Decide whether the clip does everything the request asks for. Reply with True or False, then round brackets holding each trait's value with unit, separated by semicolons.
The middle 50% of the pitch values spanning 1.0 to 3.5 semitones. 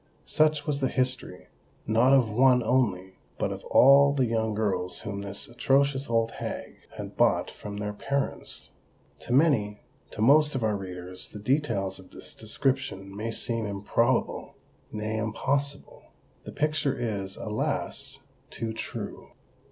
False (4.6 semitones)